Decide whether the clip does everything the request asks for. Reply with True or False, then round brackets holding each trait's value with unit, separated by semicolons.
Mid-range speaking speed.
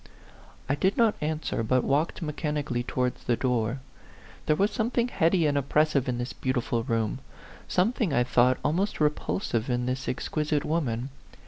True (155 wpm)